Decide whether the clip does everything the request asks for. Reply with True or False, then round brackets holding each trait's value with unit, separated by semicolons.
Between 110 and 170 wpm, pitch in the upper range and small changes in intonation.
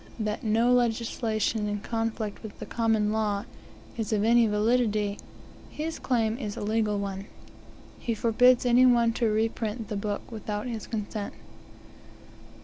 True (140 wpm; 220 Hz; 2.0 semitones)